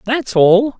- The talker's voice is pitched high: Yes, high, 225 Hz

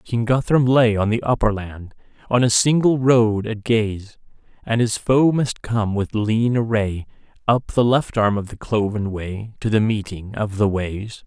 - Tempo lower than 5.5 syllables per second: Yes, 4.1 syllables/s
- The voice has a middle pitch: No, low, 110 Hz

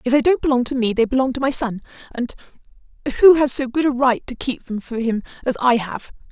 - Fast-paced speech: Yes, fast, 240 wpm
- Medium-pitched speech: No, very high, 250 Hz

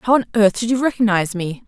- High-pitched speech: Yes, high, 215 Hz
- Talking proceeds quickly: Yes, fast, 250 wpm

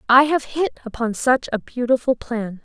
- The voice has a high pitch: Yes, high, 245 Hz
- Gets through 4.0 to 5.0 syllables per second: Yes, 4.6 syllables/s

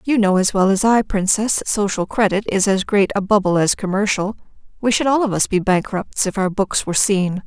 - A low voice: No, high, 200 Hz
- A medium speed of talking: No, fast, 235 wpm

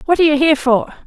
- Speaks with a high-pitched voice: Yes, very high, 295 Hz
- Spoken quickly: Yes, fast, 285 wpm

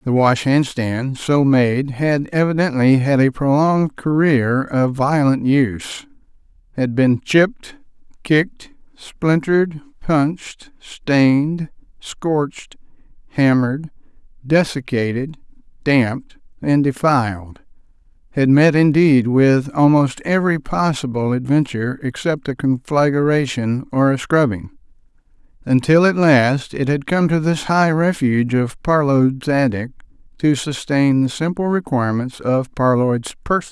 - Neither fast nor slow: No, slow, 110 wpm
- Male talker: Yes, male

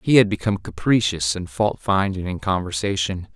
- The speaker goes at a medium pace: Yes, average, 160 wpm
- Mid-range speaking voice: No, very low, 95 Hz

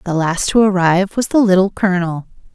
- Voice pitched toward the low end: No, high, 190 Hz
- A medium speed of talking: Yes, average, 190 wpm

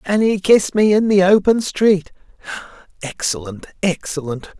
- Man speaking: Yes, male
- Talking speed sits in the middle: No, slow, 120 wpm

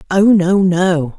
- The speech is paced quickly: No, average, 150 wpm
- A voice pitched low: No, medium, 185 Hz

